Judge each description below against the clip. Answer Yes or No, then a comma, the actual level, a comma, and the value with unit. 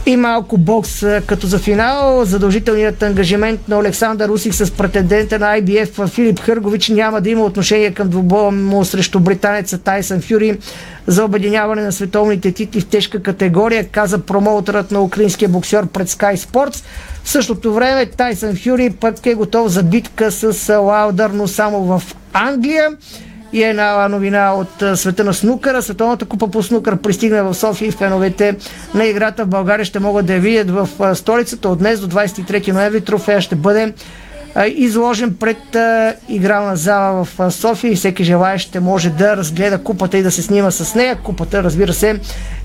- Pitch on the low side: No, high, 205 Hz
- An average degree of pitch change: No, narrow, 2.0 semitones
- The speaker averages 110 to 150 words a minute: No, fast, 165 wpm